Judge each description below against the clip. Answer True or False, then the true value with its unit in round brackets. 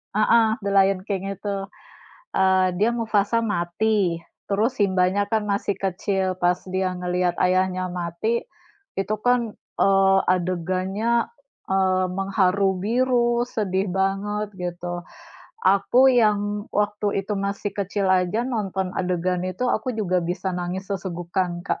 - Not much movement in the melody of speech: True (2.2 semitones)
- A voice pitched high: True (195 Hz)